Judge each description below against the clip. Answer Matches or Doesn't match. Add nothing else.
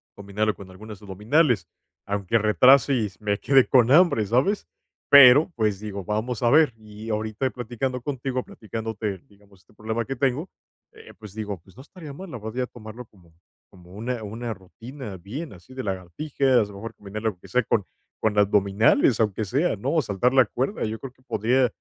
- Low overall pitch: Matches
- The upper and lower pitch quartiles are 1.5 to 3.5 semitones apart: Doesn't match